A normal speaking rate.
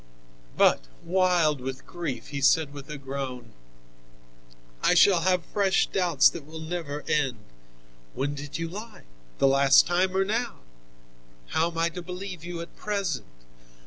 Yes: average, 150 wpm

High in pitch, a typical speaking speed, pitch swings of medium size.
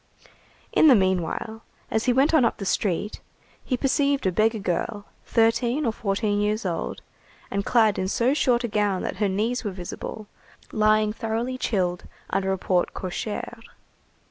Yes: high, 215 Hz; average, 165 wpm; average, 3.4 semitones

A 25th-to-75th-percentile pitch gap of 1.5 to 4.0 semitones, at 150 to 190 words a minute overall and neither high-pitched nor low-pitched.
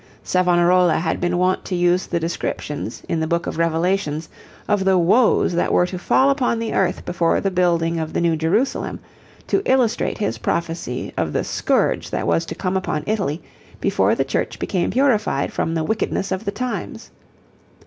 Yes: average, 3.1 semitones; average, 180 wpm; medium, 175 Hz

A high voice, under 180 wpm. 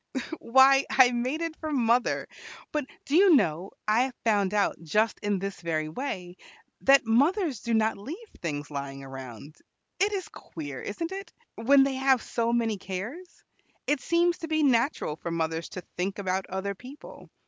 Yes: high, 230 Hz; average, 170 wpm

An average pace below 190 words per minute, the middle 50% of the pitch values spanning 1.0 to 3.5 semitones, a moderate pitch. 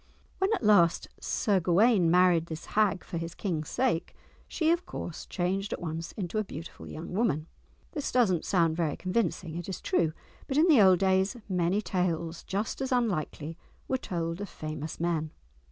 No: average, 180 wpm; average, 4.2 semitones; medium, 180 Hz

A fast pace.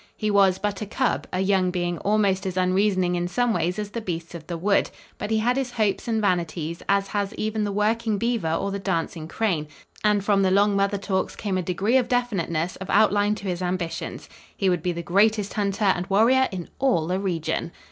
Yes: fast, 220 wpm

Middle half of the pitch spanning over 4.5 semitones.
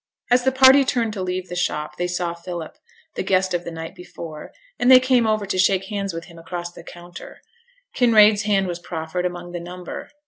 No: average, 3.4 semitones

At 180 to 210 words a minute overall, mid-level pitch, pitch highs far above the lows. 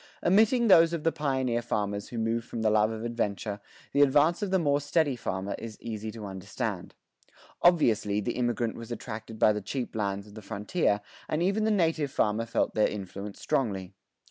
No: average, 195 wpm; low, 115 Hz; wide, 5.9 semitones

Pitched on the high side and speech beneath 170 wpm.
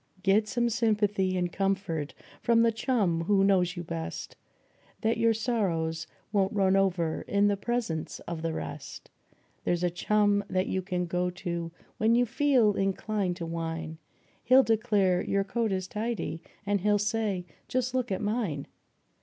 Yes: high, 195 Hz; average, 160 wpm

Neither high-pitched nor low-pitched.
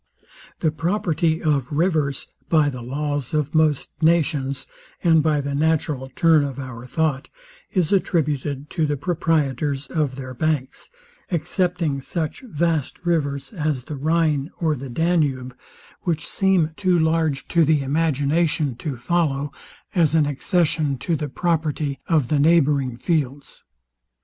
Yes: medium, 150 Hz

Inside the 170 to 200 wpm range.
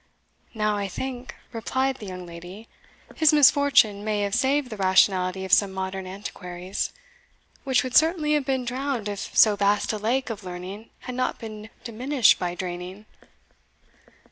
No: average, 155 wpm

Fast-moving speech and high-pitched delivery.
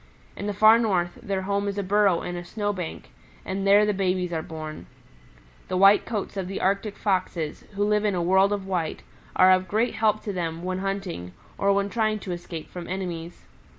Yes: fast, 210 wpm; high, 195 Hz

